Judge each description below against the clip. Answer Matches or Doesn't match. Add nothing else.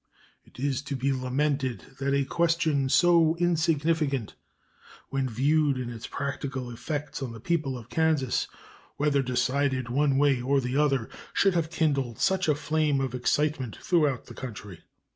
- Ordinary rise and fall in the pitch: Matches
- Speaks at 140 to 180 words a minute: Matches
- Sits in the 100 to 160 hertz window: Matches